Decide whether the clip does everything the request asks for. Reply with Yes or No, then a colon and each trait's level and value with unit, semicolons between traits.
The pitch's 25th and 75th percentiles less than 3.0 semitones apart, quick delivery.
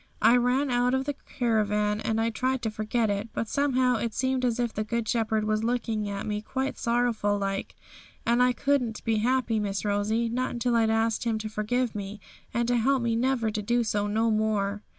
Yes: narrow, 2.4 semitones; fast, 215 wpm